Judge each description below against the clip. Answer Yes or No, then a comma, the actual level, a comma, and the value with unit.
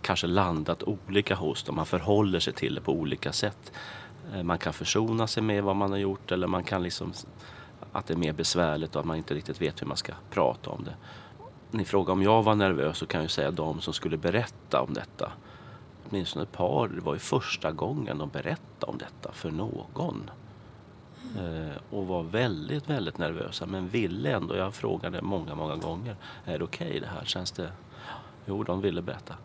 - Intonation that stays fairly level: No, average, 3.8 semitones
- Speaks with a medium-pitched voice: No, very low, 95 Hz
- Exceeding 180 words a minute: Yes, average, 200 wpm